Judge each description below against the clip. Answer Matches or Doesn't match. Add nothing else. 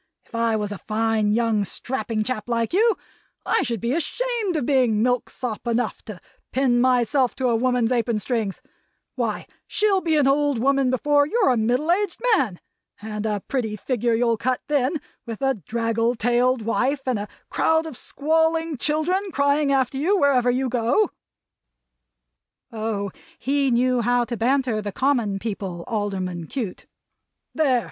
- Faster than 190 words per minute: Doesn't match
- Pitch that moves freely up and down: Doesn't match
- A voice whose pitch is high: Matches